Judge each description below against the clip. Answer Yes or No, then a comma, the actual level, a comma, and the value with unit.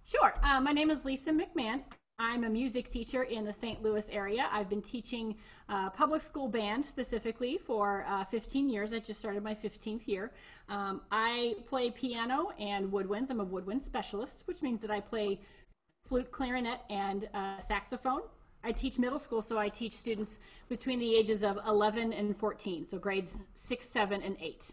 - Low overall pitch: No, high, 225 Hz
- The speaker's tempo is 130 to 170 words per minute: No, average, 180 wpm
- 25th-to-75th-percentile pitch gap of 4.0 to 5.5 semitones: No, average, 3.4 semitones